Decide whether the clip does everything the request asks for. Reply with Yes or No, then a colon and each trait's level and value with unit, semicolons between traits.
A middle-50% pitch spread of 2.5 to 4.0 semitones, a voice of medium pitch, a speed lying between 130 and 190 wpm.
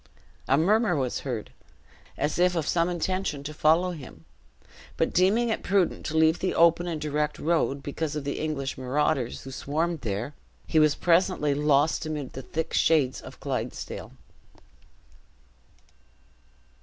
Yes: average, 3.4 semitones; medium, 155 Hz; average, 145 wpm